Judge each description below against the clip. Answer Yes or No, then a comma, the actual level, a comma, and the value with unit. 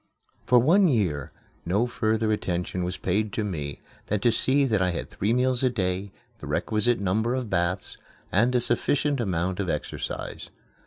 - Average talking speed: Yes, average, 170 wpm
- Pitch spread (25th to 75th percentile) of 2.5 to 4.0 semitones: No, average, 4.8 semitones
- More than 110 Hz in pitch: No, low, 105 Hz